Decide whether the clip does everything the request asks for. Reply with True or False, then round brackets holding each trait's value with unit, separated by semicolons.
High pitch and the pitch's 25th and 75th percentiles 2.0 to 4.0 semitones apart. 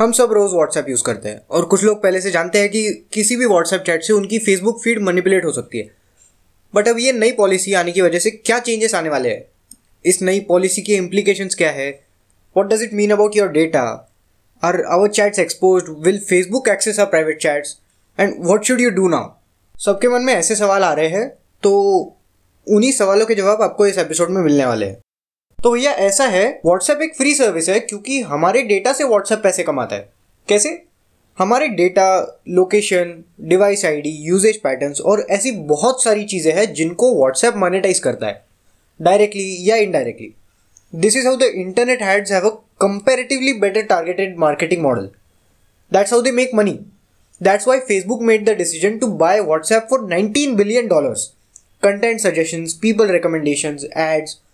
False (195 Hz; 4.7 semitones)